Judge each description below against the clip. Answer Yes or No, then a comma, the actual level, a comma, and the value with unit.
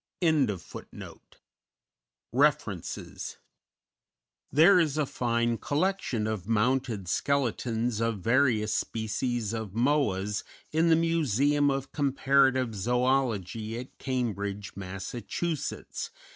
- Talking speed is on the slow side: Yes, slow, 90 wpm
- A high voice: No, low, 120 Hz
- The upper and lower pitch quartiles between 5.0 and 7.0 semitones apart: No, average, 4.5 semitones